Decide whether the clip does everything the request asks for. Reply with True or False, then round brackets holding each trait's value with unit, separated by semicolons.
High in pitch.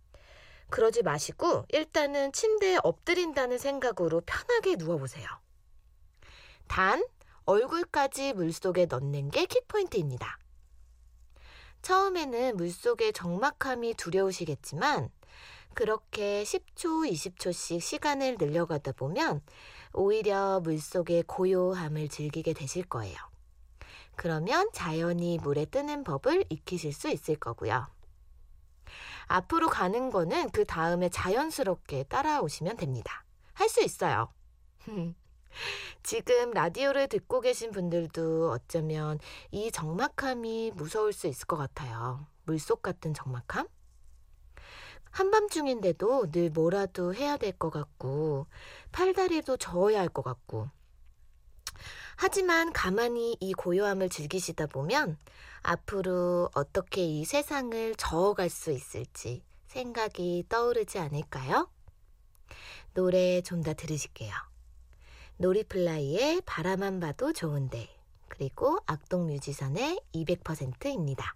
False (175 Hz)